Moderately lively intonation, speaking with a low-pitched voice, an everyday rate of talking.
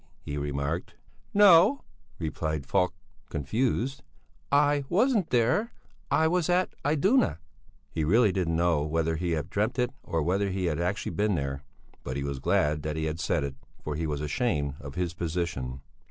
No: wide, 8.6 semitones; very low, 85 Hz; average, 170 wpm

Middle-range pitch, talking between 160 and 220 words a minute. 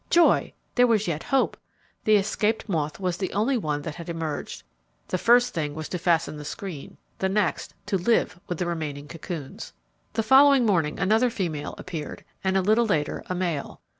Yes: medium, 180 Hz; average, 185 wpm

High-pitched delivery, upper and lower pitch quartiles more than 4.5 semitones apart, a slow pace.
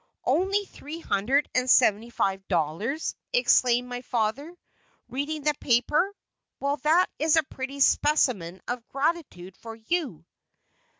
Yes: very high, 260 Hz; wide, 5.4 semitones; slow, 125 wpm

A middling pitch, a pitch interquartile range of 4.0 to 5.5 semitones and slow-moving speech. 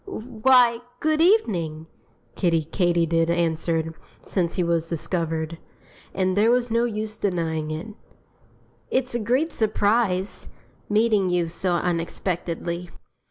Yes: medium, 180 Hz; average, 5.2 semitones; slow, 115 wpm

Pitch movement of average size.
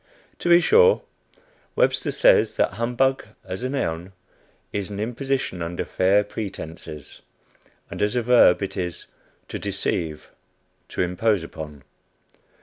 No: wide, 6.0 semitones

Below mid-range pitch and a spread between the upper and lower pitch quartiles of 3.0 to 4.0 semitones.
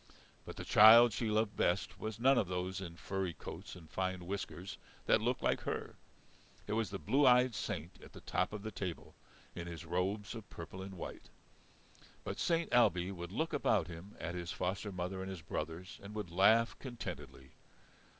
Yes: very low, 95 Hz; average, 3.7 semitones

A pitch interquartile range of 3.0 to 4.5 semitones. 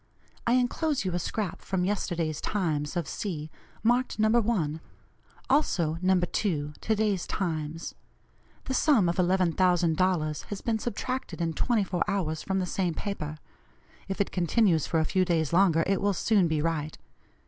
Yes: average, 4.2 semitones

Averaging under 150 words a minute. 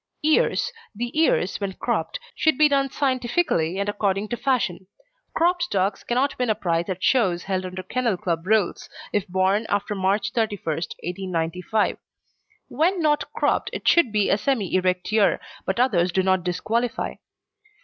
No: average, 160 wpm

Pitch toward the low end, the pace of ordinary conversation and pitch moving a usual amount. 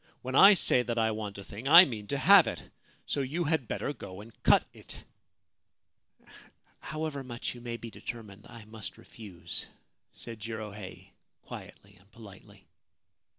Yes: low, 115 Hz; average, 165 wpm; average, 4.4 semitones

